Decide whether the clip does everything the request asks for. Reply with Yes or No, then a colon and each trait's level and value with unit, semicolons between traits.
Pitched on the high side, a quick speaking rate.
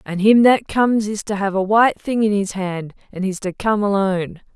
Yes: high, 205 Hz; fast, 235 wpm